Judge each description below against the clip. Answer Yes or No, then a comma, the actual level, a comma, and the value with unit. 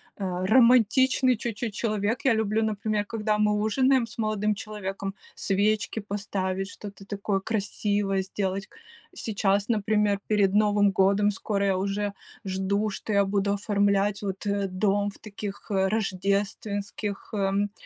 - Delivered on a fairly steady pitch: Yes, narrow, 1.4 semitones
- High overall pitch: Yes, high, 205 Hz